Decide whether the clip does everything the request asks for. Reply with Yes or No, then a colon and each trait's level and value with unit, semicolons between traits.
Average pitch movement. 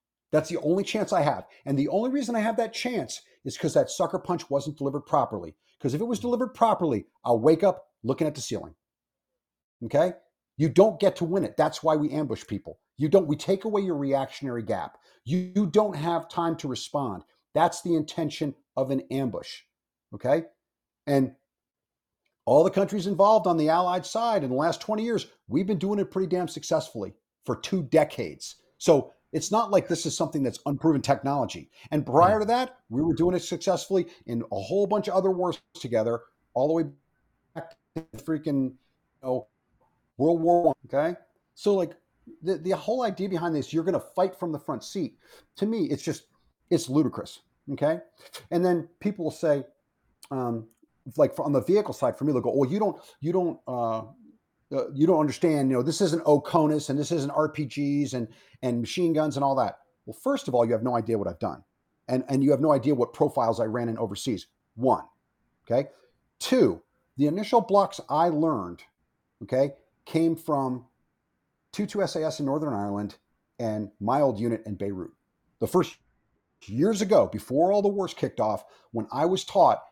No: wide, 5.7 semitones